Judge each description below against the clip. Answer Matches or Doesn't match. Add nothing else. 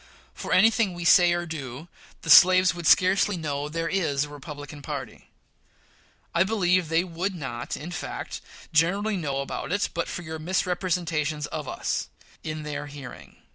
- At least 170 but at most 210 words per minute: Doesn't match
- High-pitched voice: Doesn't match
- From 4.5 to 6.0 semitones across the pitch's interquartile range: Doesn't match